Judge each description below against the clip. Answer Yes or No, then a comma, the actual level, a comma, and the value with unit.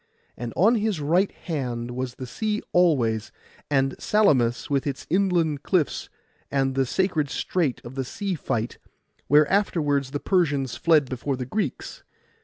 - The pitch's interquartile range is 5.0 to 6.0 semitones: Yes, wide, 5.6 semitones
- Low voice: No, medium, 145 Hz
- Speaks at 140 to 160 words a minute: Yes, average, 150 wpm